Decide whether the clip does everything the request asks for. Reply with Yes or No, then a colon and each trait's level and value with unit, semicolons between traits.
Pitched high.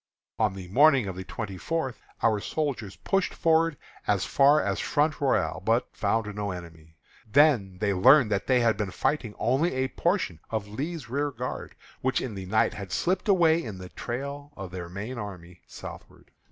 No: low, 115 Hz